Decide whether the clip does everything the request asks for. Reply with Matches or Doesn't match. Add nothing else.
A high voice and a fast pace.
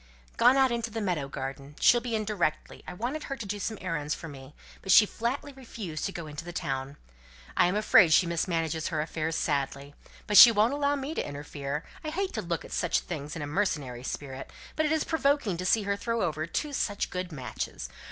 Doesn't match